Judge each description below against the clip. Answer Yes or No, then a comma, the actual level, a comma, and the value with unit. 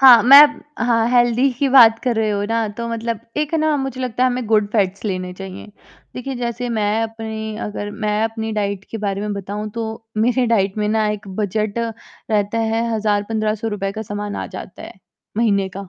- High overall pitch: Yes, high, 220 Hz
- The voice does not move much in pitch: Yes, narrow, 2.2 semitones